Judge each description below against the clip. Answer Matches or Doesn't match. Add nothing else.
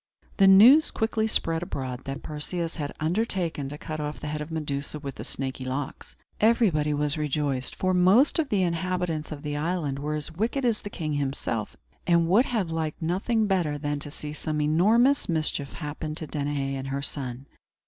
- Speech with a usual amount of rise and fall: Matches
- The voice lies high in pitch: Doesn't match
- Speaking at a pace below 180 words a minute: Doesn't match